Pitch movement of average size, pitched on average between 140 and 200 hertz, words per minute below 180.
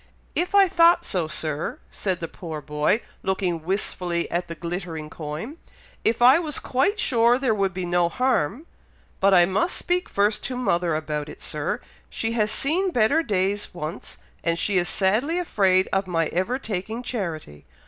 No: wide, 6.4 semitones; high, 190 Hz; average, 170 wpm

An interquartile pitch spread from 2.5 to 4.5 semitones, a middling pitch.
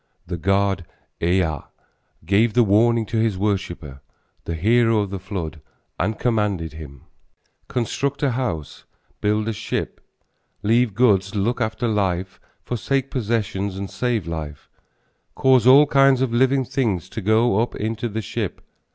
No: average, 4.0 semitones; low, 105 Hz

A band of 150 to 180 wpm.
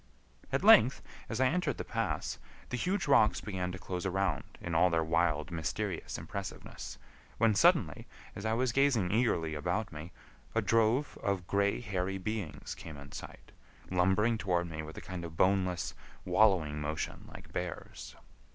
Yes: average, 160 wpm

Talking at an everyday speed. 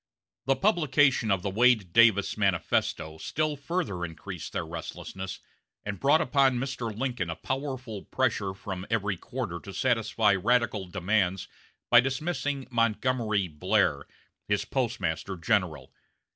No: slow, 125 wpm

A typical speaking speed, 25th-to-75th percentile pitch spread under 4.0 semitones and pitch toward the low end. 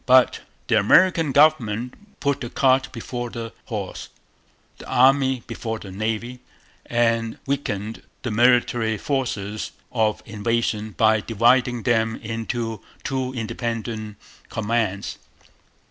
No: slow, 110 wpm; narrow, 2.6 semitones; low, 115 Hz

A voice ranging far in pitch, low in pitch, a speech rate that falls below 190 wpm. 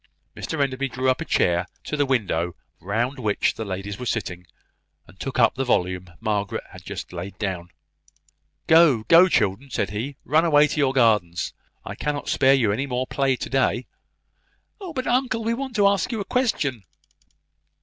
Yes: wide, 6.6 semitones; low, 130 Hz; average, 180 wpm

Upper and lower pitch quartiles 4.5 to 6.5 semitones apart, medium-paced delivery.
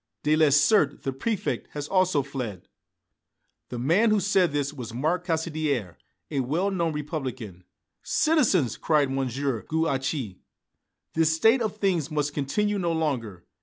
No: average, 4.8 semitones; slow, 130 wpm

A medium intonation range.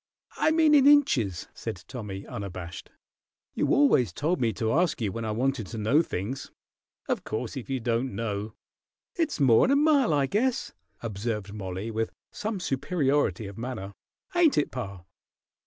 No: wide, 8.5 semitones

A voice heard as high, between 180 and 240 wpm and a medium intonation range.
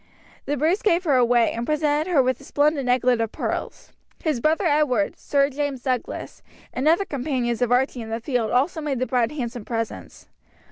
Yes: very high, 265 Hz; average, 190 wpm; average, 3.7 semitones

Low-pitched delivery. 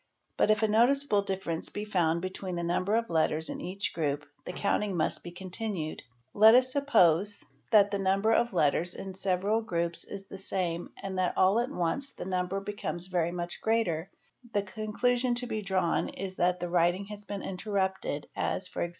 No: high, 190 Hz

